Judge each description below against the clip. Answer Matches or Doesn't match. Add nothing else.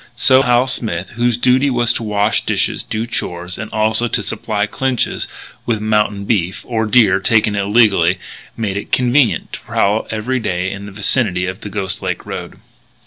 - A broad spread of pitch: Doesn't match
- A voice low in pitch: Matches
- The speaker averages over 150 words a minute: Matches